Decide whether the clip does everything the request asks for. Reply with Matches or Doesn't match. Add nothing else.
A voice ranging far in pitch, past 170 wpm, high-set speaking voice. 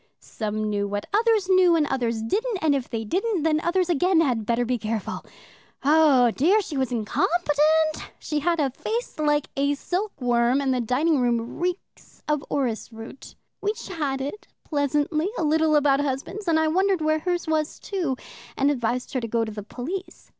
Matches